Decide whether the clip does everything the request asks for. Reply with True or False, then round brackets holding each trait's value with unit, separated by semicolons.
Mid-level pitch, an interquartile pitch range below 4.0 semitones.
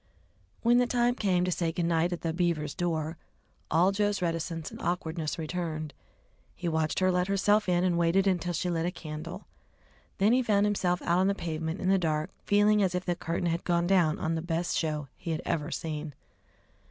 True (175 Hz; 2.6 semitones)